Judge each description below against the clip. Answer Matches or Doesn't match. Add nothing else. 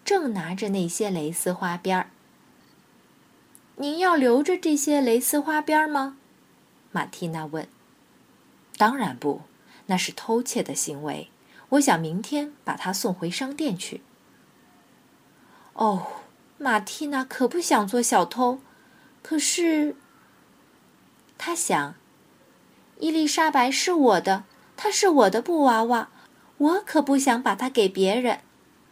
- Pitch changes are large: Matches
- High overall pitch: Matches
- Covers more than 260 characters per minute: Doesn't match